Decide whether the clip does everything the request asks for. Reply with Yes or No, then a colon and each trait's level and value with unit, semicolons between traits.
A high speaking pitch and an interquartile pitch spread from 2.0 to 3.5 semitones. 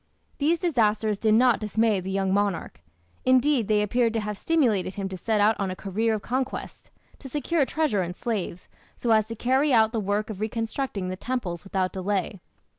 No: high, 215 Hz; average, 3.9 semitones